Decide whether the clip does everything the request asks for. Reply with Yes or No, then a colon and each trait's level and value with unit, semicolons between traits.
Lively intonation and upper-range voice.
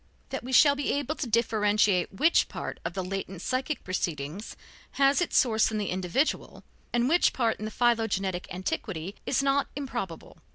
Yes: wide, 6.0 semitones; high, 220 Hz